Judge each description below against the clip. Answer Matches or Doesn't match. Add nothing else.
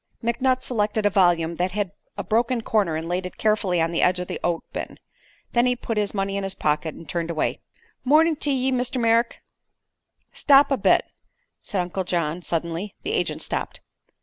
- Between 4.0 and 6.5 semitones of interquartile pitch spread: Matches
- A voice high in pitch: Matches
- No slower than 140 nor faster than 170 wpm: Doesn't match